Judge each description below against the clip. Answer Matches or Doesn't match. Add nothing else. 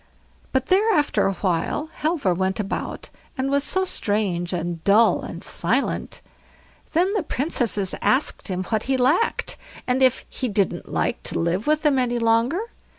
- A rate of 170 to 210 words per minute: Doesn't match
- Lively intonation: Matches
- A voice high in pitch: Matches